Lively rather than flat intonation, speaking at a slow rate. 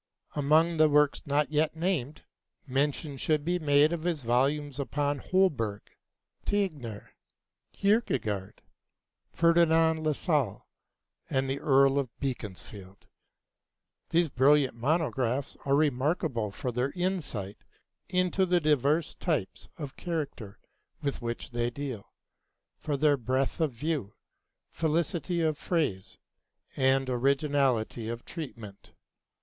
No: average, 4.2 semitones; slow, 110 wpm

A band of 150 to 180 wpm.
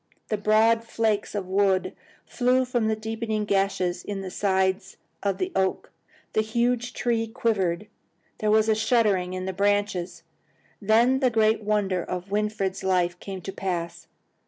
Yes: average, 155 wpm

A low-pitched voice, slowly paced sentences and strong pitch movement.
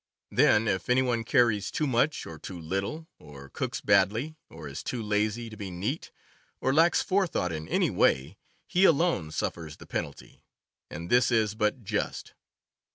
No: low, 105 Hz; average, 165 wpm; wide, 7.4 semitones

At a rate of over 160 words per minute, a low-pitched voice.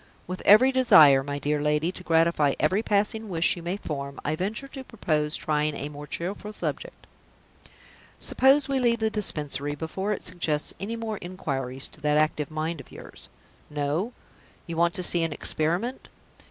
No: average, 170 wpm; medium, 170 Hz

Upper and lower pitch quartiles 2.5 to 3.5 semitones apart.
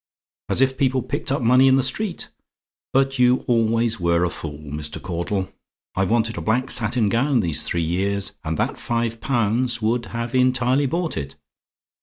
No: average, 4.9 semitones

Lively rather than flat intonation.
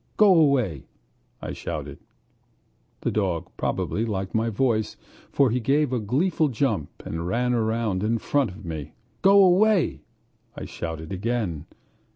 Yes: wide, 6.8 semitones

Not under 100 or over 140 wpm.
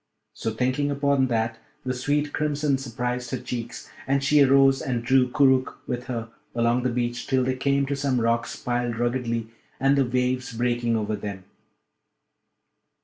No: average, 160 wpm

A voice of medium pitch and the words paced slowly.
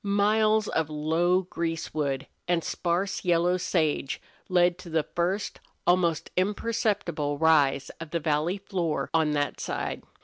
Yes: medium, 170 Hz; slow, 130 wpm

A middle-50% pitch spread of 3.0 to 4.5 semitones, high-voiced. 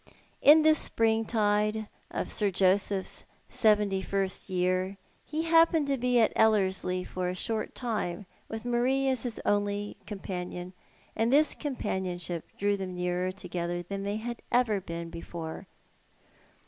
Yes: average, 3.9 semitones; high, 205 Hz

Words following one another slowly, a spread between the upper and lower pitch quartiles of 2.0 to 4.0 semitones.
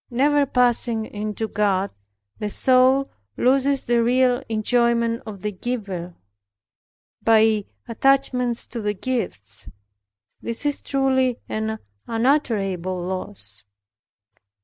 Yes: slow, 100 wpm; average, 3.6 semitones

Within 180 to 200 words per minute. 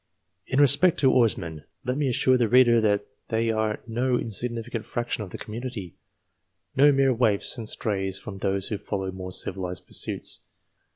No: average, 165 wpm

